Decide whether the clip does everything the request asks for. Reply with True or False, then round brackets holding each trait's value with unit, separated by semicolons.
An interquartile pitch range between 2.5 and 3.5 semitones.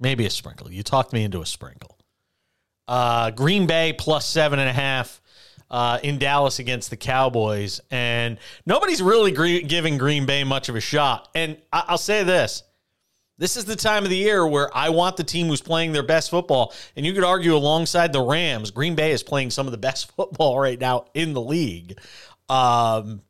False (5.1 semitones)